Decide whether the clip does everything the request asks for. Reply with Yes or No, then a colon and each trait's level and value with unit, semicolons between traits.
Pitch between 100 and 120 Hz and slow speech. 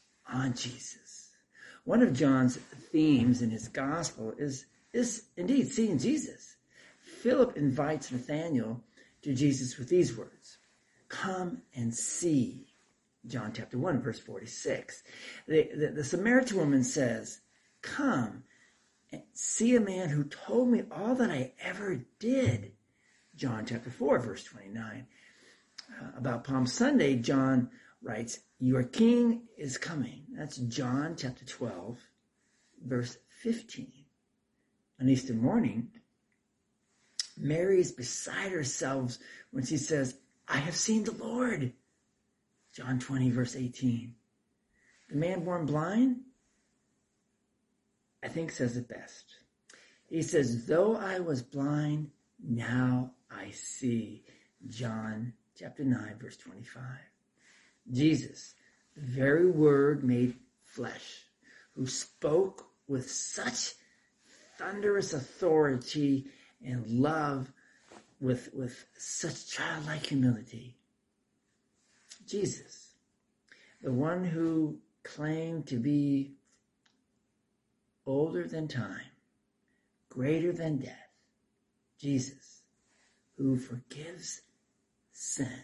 No: medium, 140 Hz; slow, 105 wpm